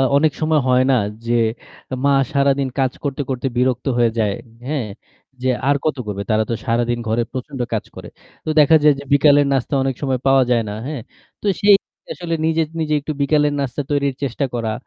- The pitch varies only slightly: No, average, 3.4 semitones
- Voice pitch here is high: No, low, 135 Hz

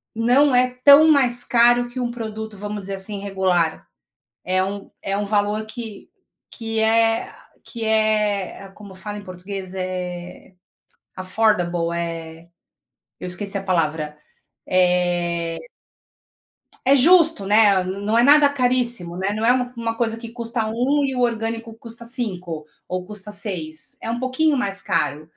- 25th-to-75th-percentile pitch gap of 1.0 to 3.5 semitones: No, average, 4.2 semitones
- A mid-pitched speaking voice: No, high, 210 Hz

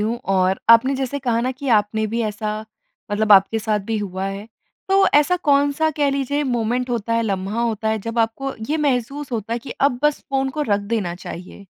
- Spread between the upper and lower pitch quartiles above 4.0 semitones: Yes, average, 4.5 semitones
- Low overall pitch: No, high, 230 Hz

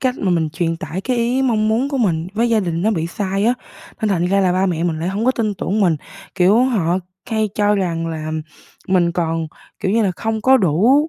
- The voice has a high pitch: Yes, high, 195 Hz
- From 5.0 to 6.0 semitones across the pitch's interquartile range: No, average, 4.6 semitones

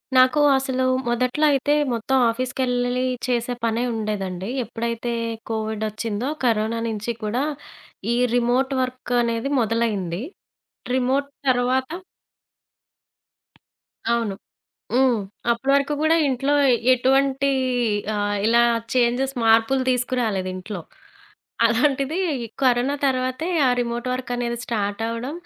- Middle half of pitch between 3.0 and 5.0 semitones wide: No, narrow, 2.5 semitones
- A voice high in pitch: Yes, high, 245 Hz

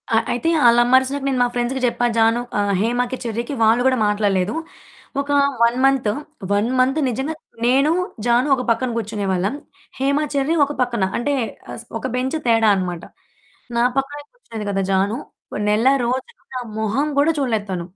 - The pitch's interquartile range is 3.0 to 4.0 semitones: Yes, average, 3.5 semitones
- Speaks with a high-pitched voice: Yes, high, 240 Hz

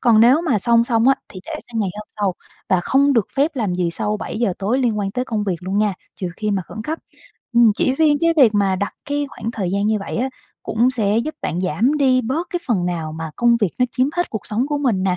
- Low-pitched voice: No, high, 225 Hz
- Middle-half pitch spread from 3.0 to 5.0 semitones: Yes, average, 4.6 semitones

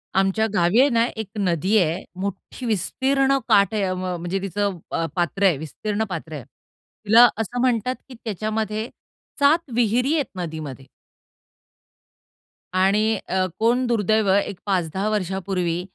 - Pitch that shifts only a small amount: No, average, 3.7 semitones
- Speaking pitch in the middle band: No, high, 200 Hz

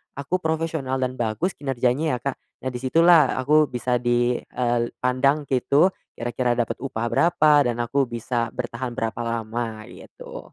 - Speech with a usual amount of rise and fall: Yes, average, 3.1 semitones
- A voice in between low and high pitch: No, low, 125 Hz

